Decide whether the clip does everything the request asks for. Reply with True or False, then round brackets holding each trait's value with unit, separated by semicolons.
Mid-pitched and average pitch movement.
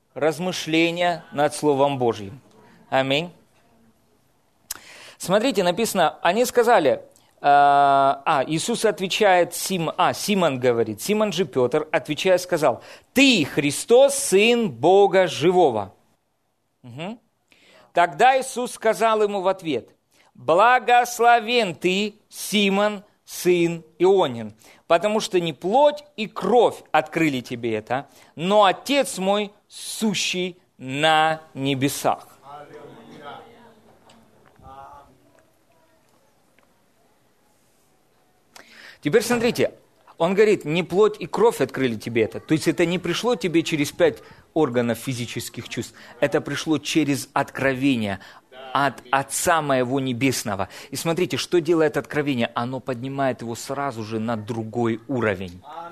False (160 Hz; 6.6 semitones)